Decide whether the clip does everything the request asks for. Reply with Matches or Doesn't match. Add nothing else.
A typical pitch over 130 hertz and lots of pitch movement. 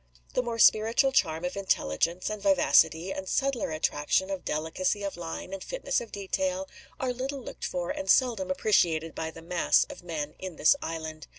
Matches